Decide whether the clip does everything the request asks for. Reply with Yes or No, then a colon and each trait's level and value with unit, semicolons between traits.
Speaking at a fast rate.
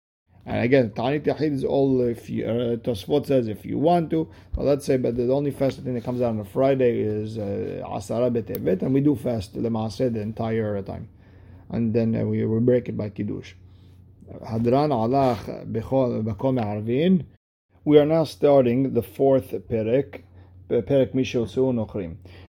No: average, 150 wpm